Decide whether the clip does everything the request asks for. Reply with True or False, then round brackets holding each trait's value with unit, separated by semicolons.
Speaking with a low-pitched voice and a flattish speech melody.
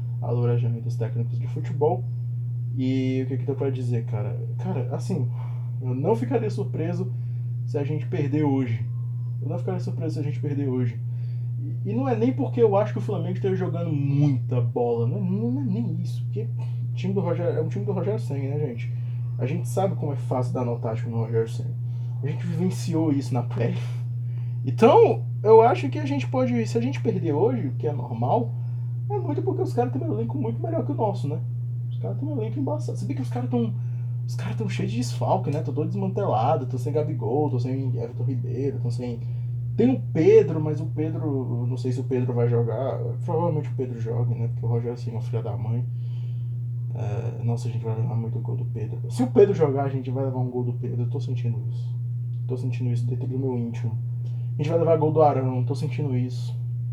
True (120 Hz; 1.0 semitones)